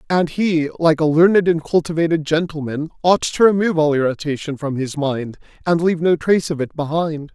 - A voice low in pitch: No, medium, 160 Hz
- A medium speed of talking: Yes, average, 190 wpm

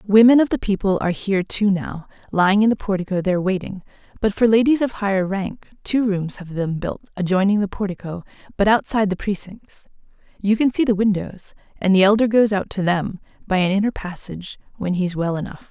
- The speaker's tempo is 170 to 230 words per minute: Yes, average, 195 wpm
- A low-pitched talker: No, high, 200 Hz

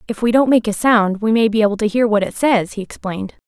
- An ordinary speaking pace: No, fast, 295 wpm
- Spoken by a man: No, female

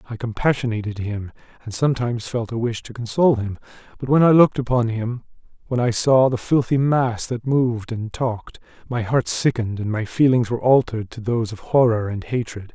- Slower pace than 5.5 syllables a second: No, 5.8 syllables/s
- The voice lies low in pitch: Yes, low, 120 Hz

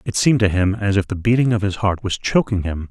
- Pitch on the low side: Yes, low, 100 Hz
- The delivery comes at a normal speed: No, fast, 290 wpm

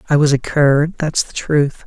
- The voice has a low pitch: No, medium, 145 Hz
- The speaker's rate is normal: No, fast, 225 wpm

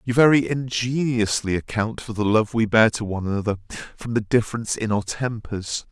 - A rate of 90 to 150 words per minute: No, average, 185 wpm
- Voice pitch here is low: Yes, low, 110 Hz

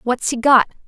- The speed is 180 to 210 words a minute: Yes, fast, 205 wpm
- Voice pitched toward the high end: Yes, very high, 250 Hz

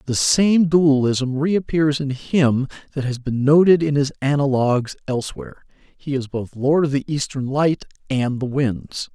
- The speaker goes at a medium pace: Yes, average, 165 wpm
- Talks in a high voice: No, medium, 140 Hz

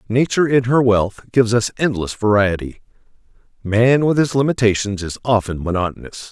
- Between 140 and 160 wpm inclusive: Yes, average, 145 wpm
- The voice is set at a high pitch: No, low, 115 Hz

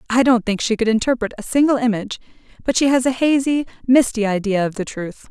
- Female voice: Yes, female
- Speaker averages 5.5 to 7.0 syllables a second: Yes, 6.1 syllables/s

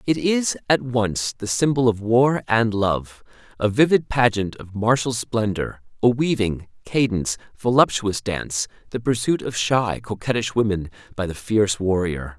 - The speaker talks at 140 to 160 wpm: Yes, average, 150 wpm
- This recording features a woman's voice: No, male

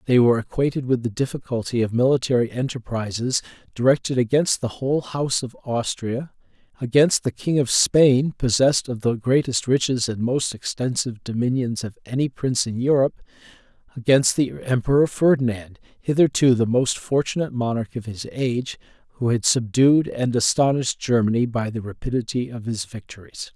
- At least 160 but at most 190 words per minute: No, average, 150 wpm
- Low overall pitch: Yes, low, 125 Hz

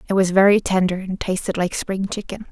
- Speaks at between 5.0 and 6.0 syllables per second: Yes, 5.6 syllables/s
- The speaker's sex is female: Yes, female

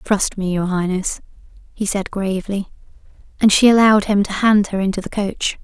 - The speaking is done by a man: No, female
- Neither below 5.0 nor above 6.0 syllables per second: Yes, 5.4 syllables/s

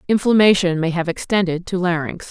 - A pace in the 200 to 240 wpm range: No, average, 155 wpm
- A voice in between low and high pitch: Yes, medium, 180 Hz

